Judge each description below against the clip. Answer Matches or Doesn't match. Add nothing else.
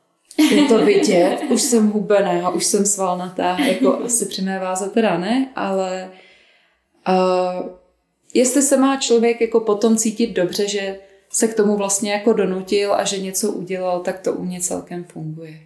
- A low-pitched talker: Doesn't match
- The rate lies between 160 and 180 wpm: Matches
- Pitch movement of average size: Matches